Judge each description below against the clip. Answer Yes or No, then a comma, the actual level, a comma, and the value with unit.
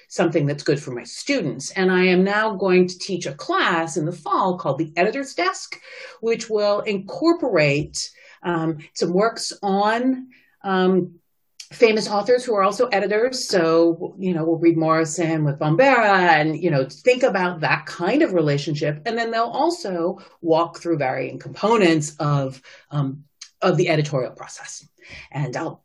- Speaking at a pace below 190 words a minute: Yes, average, 160 wpm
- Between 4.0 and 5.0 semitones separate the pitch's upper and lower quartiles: Yes, average, 4.5 semitones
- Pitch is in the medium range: Yes, medium, 175 Hz